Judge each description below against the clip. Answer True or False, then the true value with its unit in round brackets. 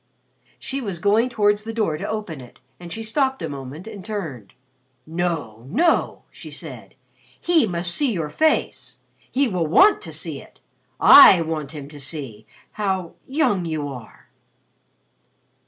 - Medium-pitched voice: True (180 Hz)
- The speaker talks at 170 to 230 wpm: False (155 wpm)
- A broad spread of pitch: True (6.6 semitones)